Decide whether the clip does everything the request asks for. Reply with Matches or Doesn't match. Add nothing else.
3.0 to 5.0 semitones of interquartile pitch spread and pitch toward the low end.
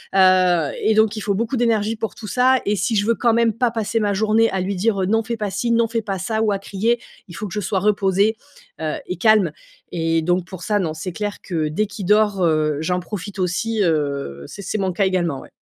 Doesn't match